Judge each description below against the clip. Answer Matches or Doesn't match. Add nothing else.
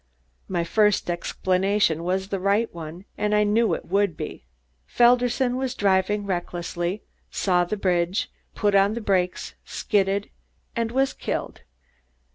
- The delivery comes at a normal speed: Doesn't match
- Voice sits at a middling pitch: Doesn't match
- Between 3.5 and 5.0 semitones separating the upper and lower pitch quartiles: Doesn't match